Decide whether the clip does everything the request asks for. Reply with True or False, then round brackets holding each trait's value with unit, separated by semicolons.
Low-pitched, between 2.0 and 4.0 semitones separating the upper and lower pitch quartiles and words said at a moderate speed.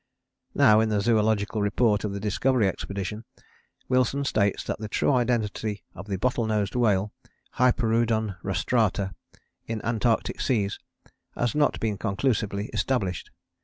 False (110 Hz; 2.8 semitones; 130 wpm)